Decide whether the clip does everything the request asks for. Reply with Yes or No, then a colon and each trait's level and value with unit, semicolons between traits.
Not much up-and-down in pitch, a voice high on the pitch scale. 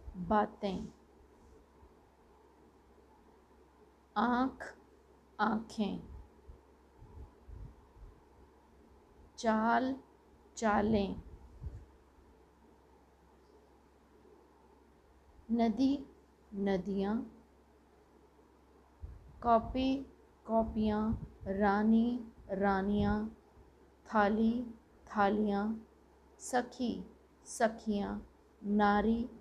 Yes: narrow, 2.2 semitones; high, 220 Hz